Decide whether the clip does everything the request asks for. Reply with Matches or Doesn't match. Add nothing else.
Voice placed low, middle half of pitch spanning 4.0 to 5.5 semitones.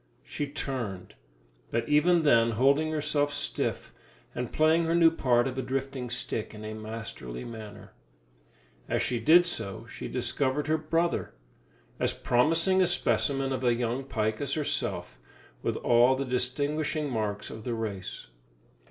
Matches